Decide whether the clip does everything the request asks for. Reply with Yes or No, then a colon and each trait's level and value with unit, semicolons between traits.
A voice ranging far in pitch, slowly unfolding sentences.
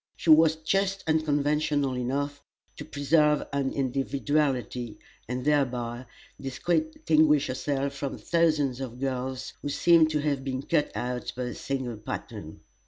No: average, 3.0 semitones; slow, 130 wpm